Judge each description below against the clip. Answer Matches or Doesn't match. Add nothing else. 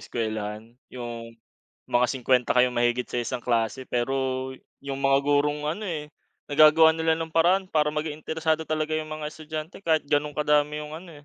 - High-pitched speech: Doesn't match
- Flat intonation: Doesn't match